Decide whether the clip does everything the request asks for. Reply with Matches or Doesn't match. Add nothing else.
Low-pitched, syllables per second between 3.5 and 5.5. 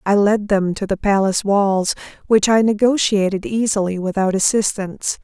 Doesn't match